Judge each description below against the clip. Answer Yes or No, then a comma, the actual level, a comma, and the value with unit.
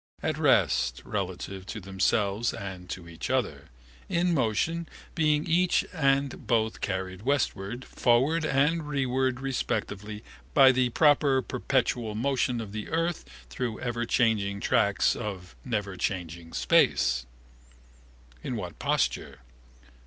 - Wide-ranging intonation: Yes, wide, 5.7 semitones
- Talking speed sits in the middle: No, slow, 115 wpm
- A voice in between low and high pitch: No, low, 120 Hz